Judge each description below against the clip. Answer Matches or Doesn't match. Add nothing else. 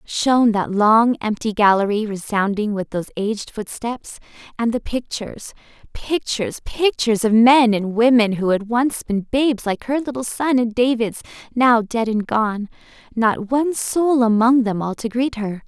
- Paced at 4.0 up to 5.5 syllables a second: Matches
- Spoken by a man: Doesn't match